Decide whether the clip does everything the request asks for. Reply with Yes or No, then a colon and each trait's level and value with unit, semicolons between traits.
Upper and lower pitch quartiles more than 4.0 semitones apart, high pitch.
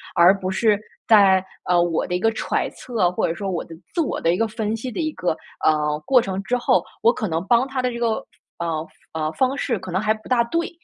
Yes: average, 5.2 semitones; high, 205 Hz